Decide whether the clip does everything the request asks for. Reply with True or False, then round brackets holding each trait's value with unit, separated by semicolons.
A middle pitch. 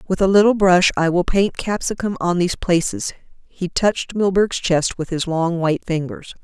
True (180 Hz)